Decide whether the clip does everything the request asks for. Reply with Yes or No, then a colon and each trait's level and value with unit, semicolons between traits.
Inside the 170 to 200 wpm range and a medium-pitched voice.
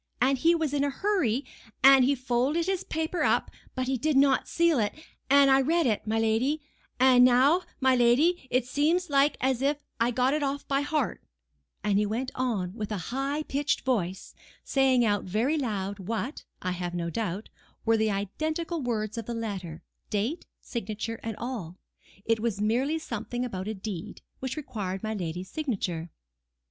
No: average, 180 wpm; high, 245 Hz